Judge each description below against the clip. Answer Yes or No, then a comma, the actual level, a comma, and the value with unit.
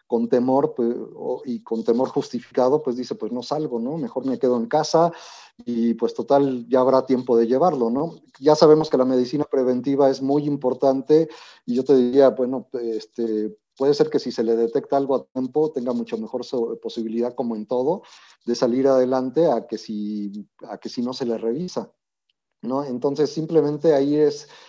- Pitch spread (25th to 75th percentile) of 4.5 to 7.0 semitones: No, average, 3.2 semitones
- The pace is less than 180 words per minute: No, average, 185 wpm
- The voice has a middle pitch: No, low, 130 Hz